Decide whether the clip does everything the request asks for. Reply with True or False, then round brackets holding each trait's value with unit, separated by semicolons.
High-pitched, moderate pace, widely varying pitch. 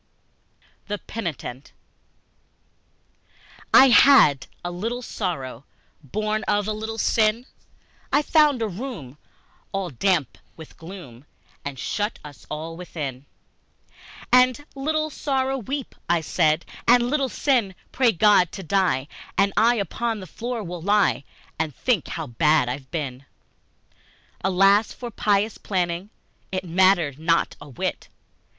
False (195 Hz; 125 wpm; 6.6 semitones)